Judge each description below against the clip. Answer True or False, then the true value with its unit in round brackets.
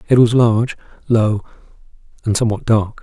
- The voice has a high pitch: False (115 Hz)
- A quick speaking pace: False (140 wpm)